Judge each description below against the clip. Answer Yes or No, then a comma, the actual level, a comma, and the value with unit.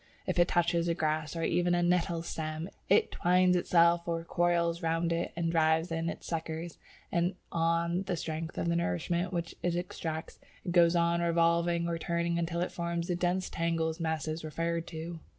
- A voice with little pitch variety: Yes, narrow, 0.9 semitones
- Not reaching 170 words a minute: No, average, 180 wpm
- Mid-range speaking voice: Yes, medium, 170 Hz